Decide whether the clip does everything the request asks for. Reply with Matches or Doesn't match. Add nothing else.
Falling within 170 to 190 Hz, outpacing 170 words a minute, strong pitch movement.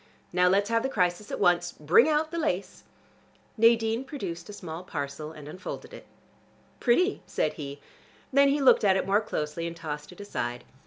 Matches